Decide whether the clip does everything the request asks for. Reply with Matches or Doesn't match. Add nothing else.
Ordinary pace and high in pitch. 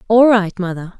Matches